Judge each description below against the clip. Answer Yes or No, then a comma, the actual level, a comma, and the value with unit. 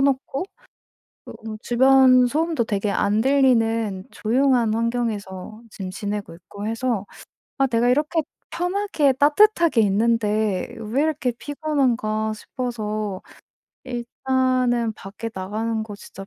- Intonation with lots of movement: No, average, 3.8 semitones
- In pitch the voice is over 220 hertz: Yes, high, 230 Hz